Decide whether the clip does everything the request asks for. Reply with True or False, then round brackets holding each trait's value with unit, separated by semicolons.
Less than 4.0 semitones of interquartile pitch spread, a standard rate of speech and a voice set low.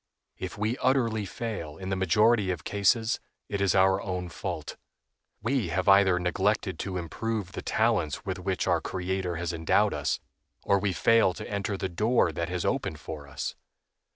True (3.1 semitones; 175 wpm; 95 Hz)